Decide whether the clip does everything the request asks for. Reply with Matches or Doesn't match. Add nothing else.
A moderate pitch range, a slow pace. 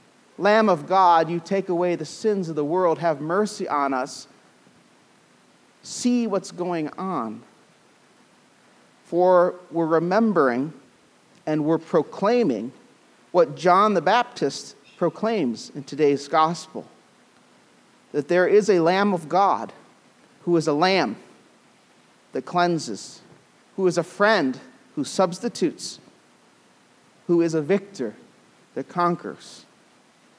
Matches